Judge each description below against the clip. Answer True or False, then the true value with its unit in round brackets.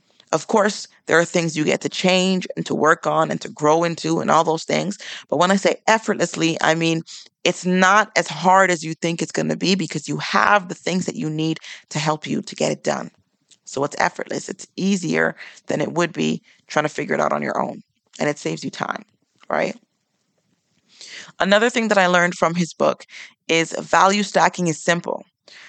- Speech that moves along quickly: True (210 wpm)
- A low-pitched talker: False (175 Hz)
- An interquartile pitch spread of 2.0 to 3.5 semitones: True (2.9 semitones)